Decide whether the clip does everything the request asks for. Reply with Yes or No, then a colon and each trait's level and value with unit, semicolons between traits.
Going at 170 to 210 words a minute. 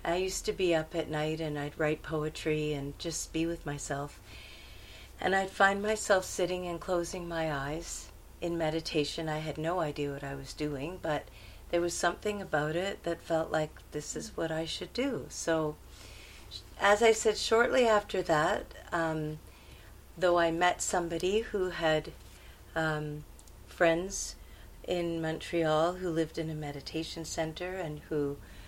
No: average, 160 wpm